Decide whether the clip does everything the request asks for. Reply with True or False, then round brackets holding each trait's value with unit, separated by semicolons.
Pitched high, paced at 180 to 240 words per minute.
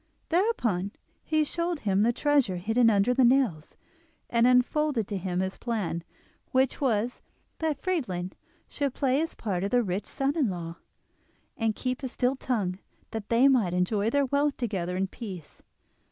False (235 Hz; 165 wpm)